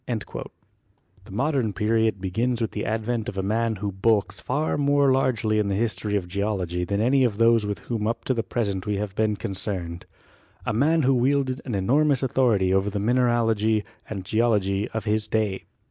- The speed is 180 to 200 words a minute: Yes, average, 190 wpm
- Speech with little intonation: No, average, 3.3 semitones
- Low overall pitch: Yes, low, 110 Hz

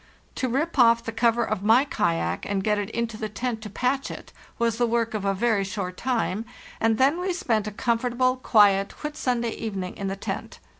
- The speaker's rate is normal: No, fast, 210 wpm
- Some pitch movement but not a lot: Yes, average, 3.4 semitones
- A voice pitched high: Yes, high, 225 Hz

